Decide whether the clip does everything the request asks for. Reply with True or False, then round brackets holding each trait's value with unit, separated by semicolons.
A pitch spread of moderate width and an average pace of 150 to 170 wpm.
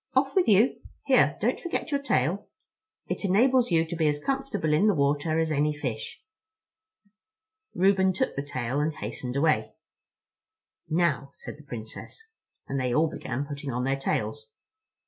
False (6.0 semitones; 160 wpm)